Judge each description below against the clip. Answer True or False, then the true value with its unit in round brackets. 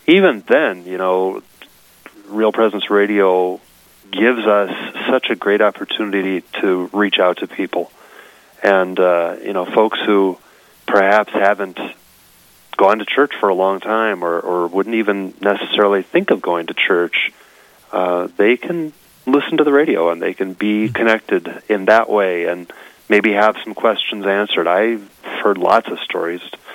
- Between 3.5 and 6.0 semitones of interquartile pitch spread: False (2.9 semitones)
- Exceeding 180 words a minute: False (155 wpm)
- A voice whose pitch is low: True (100 Hz)